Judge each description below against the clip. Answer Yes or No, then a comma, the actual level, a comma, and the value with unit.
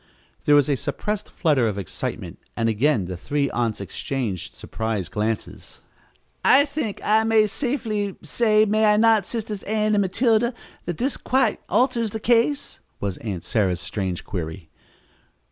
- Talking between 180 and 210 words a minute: No, average, 155 wpm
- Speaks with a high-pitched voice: Yes, high, 195 Hz